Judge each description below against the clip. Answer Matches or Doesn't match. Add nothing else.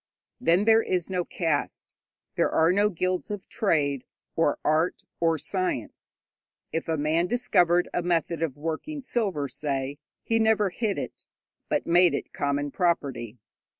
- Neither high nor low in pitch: Matches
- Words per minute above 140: Matches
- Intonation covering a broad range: Doesn't match